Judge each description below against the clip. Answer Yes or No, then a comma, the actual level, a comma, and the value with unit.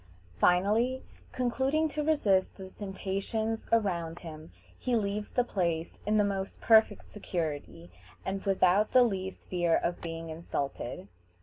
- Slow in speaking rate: Yes, slow, 130 wpm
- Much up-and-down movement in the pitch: No, average, 4.5 semitones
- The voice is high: Yes, high, 195 Hz